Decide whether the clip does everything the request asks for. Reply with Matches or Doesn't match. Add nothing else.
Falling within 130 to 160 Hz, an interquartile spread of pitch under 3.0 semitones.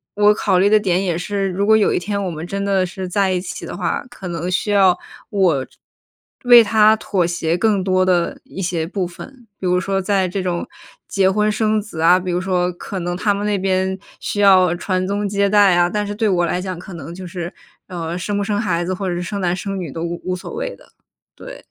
Doesn't match